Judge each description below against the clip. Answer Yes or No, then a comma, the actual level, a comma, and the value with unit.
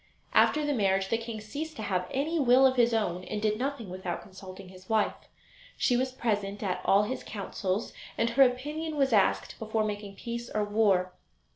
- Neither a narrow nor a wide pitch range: Yes, average, 4.5 semitones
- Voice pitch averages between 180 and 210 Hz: No, high, 220 Hz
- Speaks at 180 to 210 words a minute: Yes, average, 190 wpm